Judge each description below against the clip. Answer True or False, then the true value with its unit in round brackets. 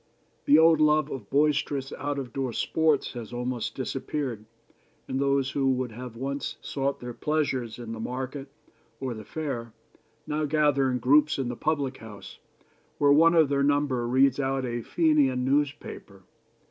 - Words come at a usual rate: True (160 wpm)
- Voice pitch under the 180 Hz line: True (135 Hz)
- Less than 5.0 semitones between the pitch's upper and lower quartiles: True (2.8 semitones)